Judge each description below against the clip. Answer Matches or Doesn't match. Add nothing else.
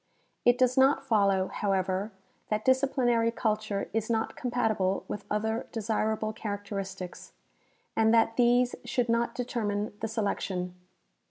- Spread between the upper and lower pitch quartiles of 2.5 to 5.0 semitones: Matches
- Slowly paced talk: Matches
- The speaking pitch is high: Matches